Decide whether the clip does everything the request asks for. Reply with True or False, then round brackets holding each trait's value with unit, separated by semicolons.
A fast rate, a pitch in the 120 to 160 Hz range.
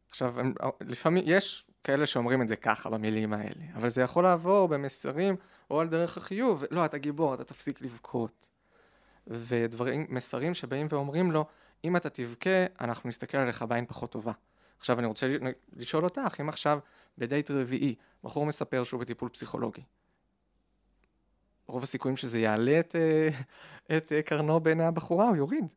True (160 wpm; 140 Hz)